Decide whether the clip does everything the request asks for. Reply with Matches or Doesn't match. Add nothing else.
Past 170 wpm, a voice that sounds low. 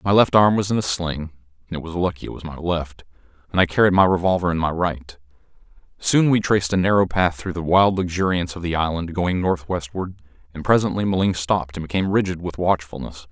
Matches